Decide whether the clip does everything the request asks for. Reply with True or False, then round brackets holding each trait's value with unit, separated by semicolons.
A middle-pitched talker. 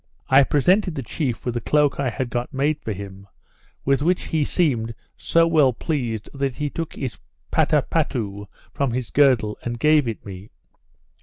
False (130 Hz)